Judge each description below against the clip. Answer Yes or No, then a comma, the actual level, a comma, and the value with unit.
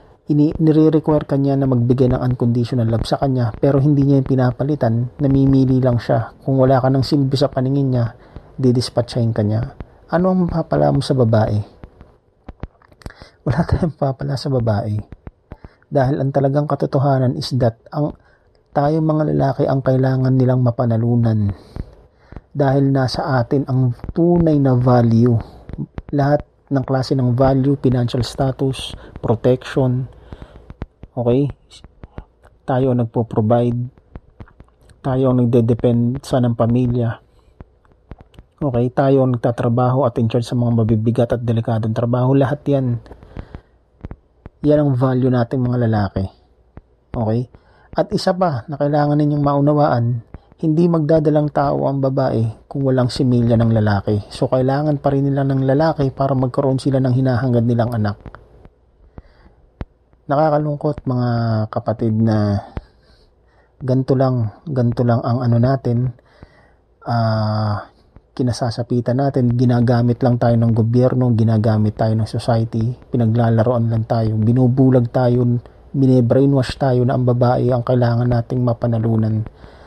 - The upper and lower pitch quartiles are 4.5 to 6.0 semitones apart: No, average, 3.0 semitones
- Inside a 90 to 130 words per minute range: Yes, average, 125 wpm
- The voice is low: Yes, low, 125 Hz